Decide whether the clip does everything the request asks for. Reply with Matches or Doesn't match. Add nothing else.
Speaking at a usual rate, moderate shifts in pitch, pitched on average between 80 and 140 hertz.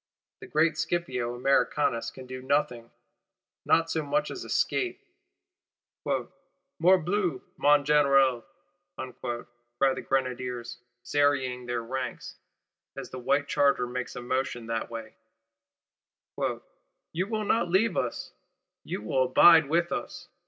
Doesn't match